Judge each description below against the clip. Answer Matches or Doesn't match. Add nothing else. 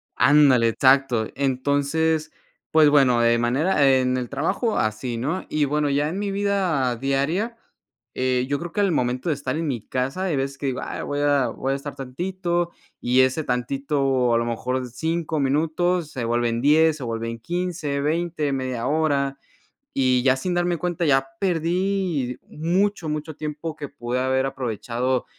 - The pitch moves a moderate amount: Matches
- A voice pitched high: Doesn't match